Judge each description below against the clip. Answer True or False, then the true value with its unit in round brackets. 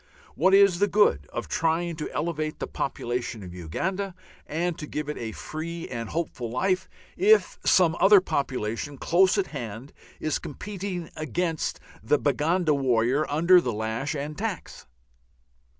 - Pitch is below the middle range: False (155 Hz)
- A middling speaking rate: True (145 wpm)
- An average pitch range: False (6.0 semitones)